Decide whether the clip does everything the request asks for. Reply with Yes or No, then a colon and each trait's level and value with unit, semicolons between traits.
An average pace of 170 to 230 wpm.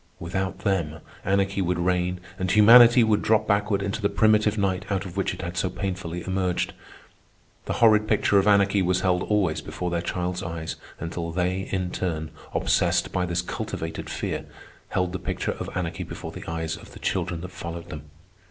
Yes: average, 185 wpm